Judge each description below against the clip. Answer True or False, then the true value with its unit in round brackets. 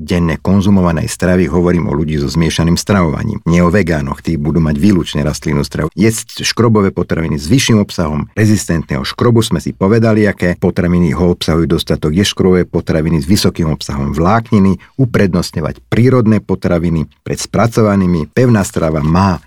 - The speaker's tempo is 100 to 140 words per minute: False (150 wpm)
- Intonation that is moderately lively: True (4.2 semitones)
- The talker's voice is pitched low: True (90 Hz)